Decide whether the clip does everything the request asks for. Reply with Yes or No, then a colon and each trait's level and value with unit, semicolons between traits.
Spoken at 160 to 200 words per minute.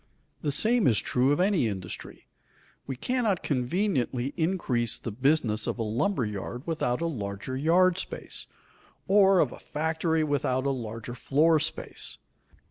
No: average, 145 wpm